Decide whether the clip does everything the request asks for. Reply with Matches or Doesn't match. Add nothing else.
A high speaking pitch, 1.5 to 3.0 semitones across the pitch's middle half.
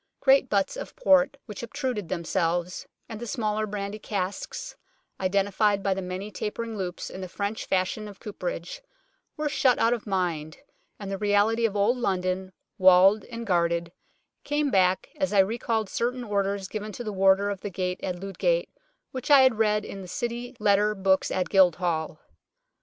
Doesn't match